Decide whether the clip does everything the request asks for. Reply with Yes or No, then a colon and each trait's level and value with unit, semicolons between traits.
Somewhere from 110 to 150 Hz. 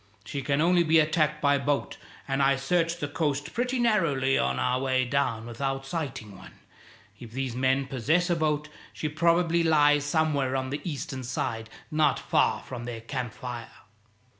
Yes: medium, 140 Hz